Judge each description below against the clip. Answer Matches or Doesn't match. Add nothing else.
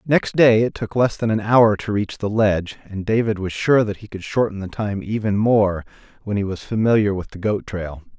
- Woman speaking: Doesn't match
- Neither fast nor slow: Doesn't match